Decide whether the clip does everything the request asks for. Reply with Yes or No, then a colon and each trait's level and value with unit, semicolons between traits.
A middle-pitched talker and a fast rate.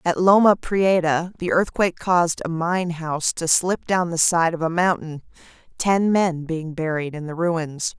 No: medium, 170 Hz; average, 180 wpm